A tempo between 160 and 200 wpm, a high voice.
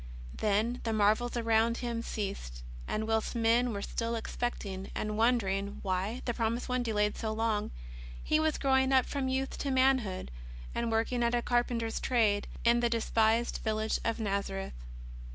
Yes: average, 165 wpm; high, 230 Hz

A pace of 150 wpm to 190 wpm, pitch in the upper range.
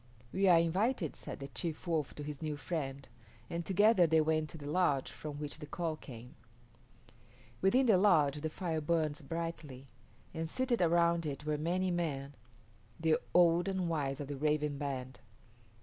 No: average, 170 wpm; medium, 160 Hz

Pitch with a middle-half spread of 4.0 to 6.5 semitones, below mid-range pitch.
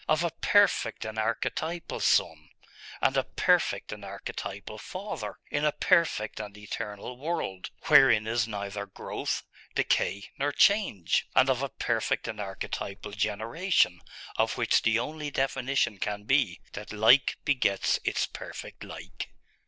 Yes: wide, 5.4 semitones; low, 115 Hz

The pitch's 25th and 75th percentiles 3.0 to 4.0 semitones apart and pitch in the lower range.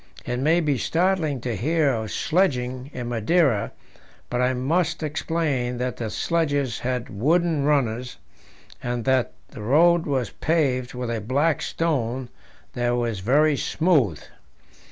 No: average, 4.6 semitones; low, 130 Hz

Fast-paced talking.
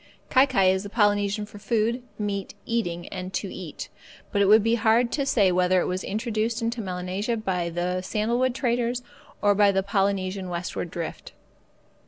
No: average, 175 wpm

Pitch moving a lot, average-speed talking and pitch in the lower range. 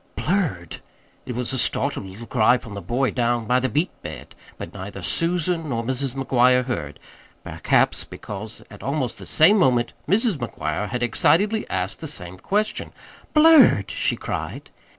Yes: wide, 6.0 semitones; average, 160 wpm; low, 125 Hz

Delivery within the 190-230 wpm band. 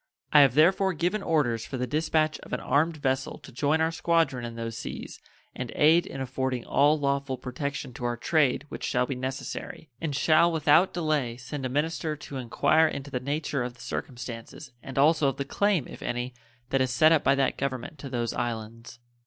Yes: average, 200 wpm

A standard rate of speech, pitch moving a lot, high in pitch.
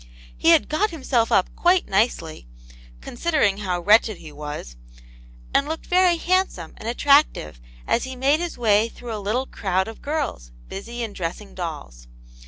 Yes: average, 160 wpm; wide, 8.3 semitones; high, 225 Hz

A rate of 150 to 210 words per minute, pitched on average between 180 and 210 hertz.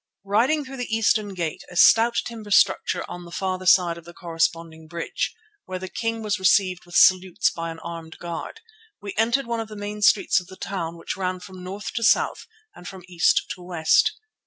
Yes: fast, 205 wpm; medium, 185 Hz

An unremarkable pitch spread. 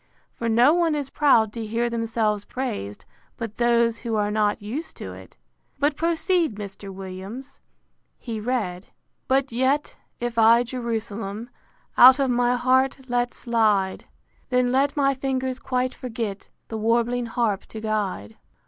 Yes: average, 3.2 semitones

